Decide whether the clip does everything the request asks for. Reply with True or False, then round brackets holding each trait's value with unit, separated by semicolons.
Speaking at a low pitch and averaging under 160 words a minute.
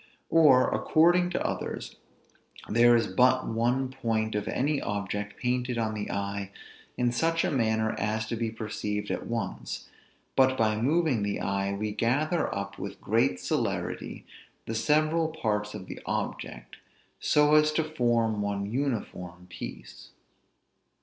True (115 Hz; 145 wpm)